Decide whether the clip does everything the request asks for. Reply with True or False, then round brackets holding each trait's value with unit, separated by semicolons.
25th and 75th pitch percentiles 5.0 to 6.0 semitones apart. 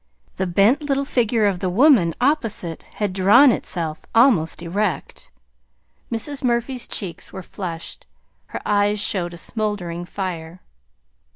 True (5.3 semitones)